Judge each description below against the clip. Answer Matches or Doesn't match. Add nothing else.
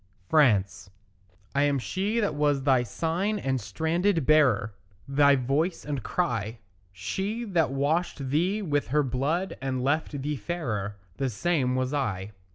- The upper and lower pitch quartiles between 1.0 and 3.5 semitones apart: Doesn't match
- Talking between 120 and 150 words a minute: Matches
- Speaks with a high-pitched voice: Doesn't match